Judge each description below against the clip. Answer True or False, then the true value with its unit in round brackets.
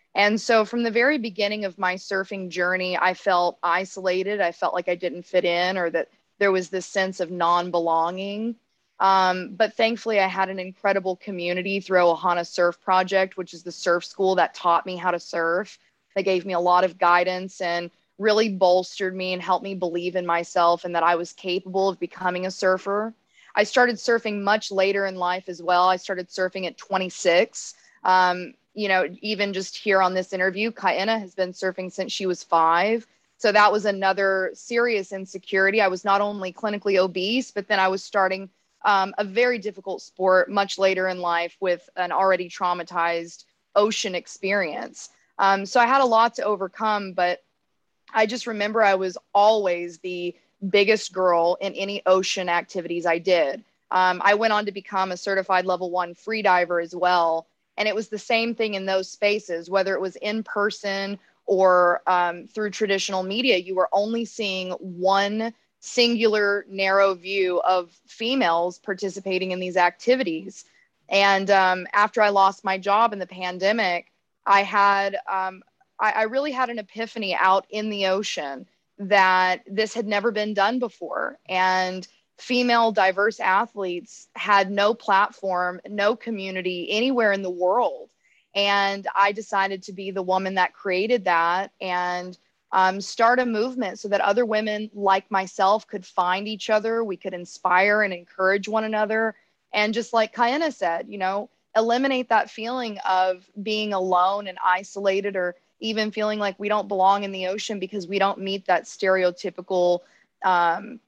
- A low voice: False (195 Hz)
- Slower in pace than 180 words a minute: True (170 wpm)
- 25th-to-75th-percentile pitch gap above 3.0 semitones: False (2.5 semitones)